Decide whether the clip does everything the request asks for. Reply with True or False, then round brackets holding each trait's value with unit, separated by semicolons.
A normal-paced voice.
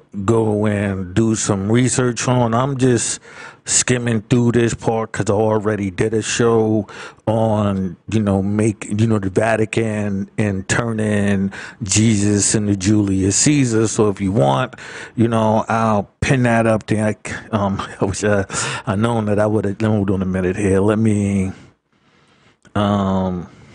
True (155 wpm)